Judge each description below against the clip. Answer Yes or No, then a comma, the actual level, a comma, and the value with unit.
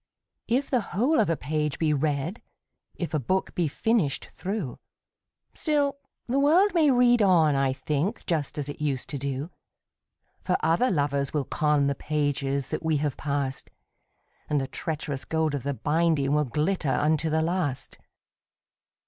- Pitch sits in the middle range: Yes, medium, 155 Hz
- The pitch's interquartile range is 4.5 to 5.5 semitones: Yes, average, 4.9 semitones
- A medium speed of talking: Yes, average, 165 wpm